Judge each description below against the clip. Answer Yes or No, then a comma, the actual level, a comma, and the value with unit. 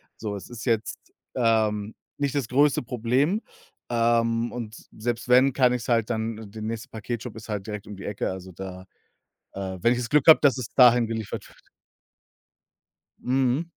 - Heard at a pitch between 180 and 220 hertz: No, low, 115 Hz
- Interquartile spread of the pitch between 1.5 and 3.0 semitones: Yes, narrow, 2.5 semitones